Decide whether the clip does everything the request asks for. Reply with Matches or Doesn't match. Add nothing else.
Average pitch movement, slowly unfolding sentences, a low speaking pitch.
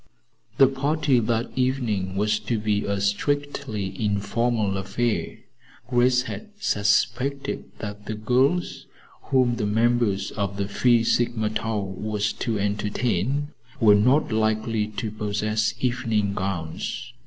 Matches